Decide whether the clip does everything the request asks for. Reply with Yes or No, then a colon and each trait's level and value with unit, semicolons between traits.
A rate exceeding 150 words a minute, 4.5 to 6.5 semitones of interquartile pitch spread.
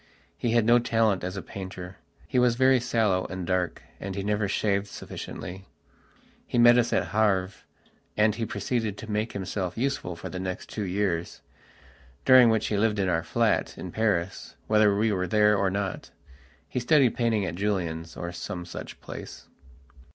No: average, 175 wpm; average, 3.4 semitones